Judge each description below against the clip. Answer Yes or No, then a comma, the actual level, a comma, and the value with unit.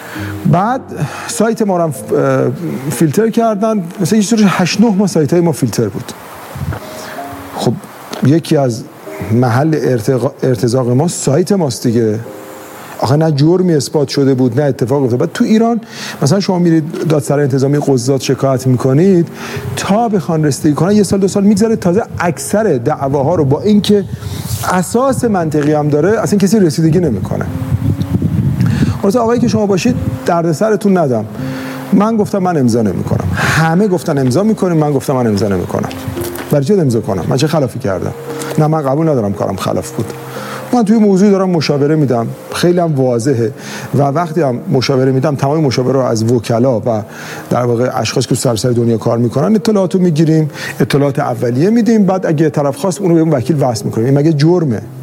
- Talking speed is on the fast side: Yes, fast, 165 wpm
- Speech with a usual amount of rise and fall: No, wide, 6.2 semitones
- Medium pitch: Yes, medium, 150 Hz